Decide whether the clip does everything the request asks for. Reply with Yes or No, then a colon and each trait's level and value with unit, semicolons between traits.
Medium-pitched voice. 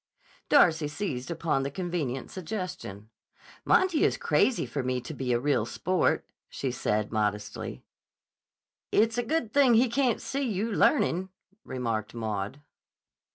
Yes: medium, 160 Hz